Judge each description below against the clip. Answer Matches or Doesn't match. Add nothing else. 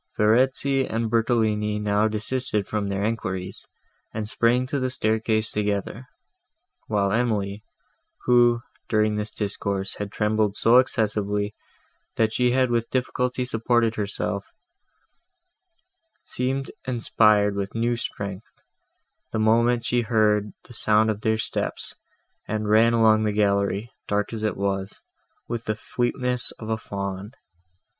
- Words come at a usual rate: Doesn't match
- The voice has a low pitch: Matches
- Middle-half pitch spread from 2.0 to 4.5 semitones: Matches